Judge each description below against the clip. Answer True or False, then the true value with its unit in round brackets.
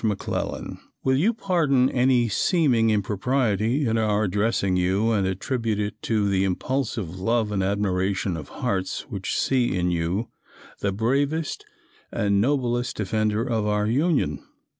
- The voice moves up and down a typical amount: True (4.3 semitones)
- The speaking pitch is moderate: False (110 Hz)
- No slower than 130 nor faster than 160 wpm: True (140 wpm)